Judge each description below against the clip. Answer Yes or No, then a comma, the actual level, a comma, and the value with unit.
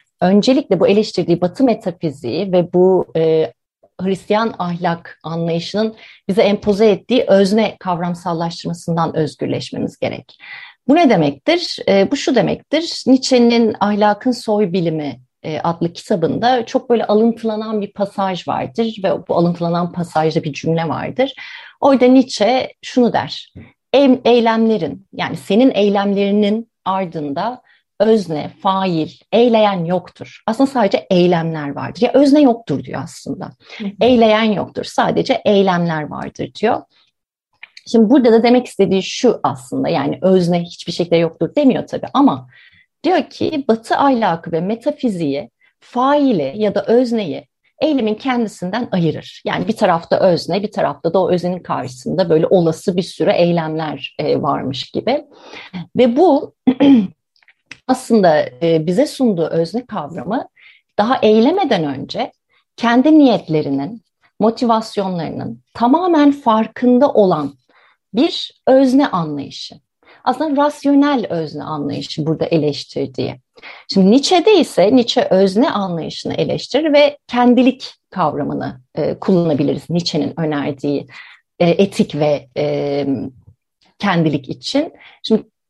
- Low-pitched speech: No, high, 200 Hz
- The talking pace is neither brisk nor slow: Yes, average, 115 wpm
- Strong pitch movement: Yes, wide, 6.6 semitones